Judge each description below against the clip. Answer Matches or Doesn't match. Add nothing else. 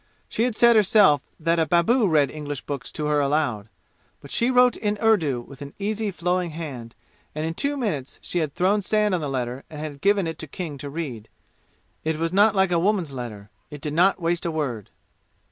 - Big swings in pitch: Matches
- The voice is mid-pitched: Matches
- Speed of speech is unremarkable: Doesn't match